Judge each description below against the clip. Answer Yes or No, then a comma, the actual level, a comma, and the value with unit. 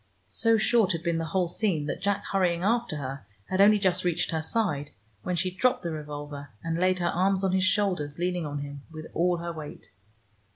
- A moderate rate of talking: No, fast, 210 wpm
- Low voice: No, medium, 175 Hz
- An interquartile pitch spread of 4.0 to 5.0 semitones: No, average, 3.5 semitones